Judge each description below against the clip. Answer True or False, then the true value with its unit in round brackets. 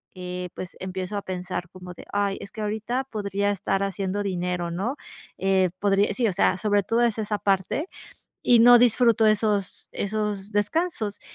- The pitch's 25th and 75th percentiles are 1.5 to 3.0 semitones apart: True (2.5 semitones)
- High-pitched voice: True (200 Hz)